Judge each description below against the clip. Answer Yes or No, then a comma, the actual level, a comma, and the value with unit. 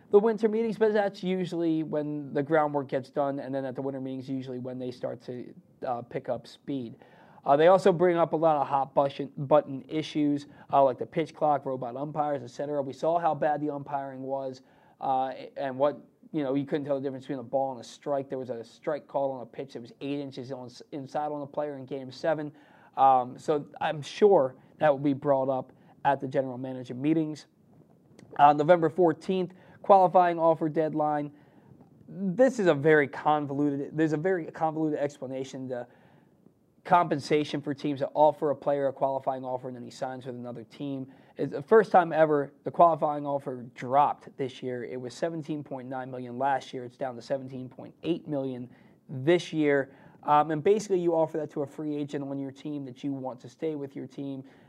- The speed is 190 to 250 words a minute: Yes, average, 200 wpm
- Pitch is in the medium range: Yes, medium, 145 Hz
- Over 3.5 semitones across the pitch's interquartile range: No, average, 2.8 semitones